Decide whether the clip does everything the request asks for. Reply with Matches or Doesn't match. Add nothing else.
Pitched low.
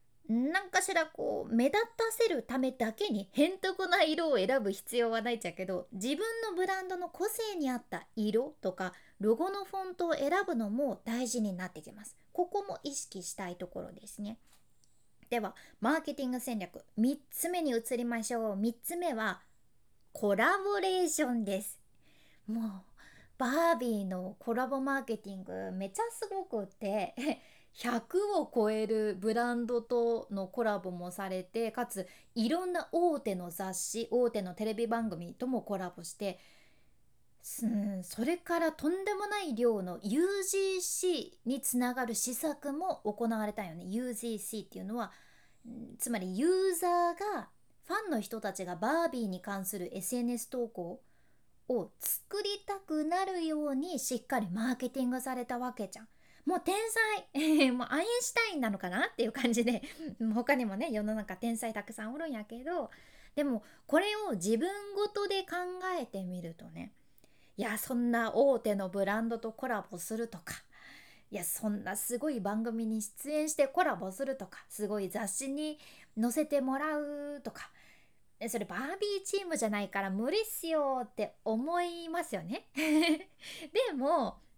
Doesn't match